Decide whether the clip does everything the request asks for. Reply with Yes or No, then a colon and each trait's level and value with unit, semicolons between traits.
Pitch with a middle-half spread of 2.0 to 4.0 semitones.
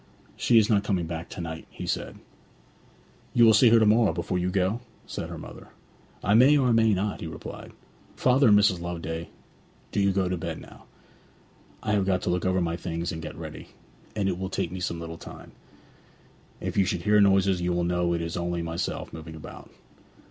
Yes: average, 3.4 semitones